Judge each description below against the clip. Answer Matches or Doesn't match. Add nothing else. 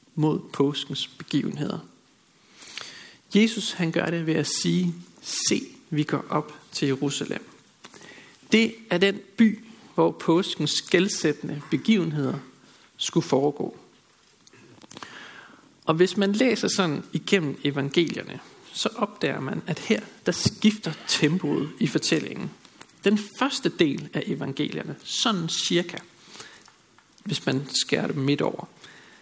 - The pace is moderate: Doesn't match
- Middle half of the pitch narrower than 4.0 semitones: Doesn't match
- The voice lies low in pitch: Doesn't match